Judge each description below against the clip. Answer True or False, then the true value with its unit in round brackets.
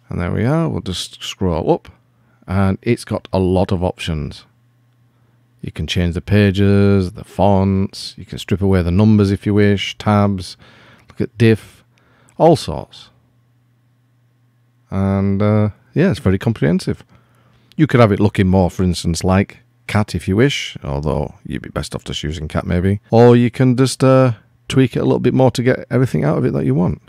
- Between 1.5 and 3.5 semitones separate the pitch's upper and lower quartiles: False (4.0 semitones)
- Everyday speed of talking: True (190 wpm)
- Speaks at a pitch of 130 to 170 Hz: False (105 Hz)